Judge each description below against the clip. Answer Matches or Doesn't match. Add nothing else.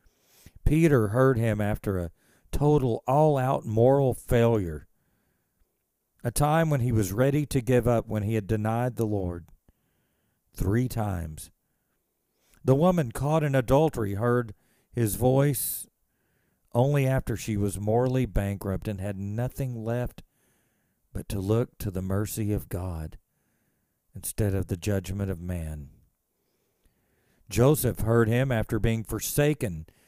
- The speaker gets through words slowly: Matches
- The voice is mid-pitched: Doesn't match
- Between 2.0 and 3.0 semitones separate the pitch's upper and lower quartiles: Doesn't match